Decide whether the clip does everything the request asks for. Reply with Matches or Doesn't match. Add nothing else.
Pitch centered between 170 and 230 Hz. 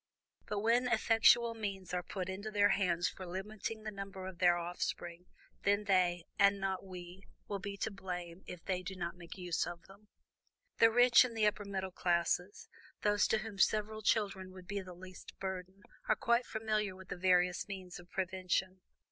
Matches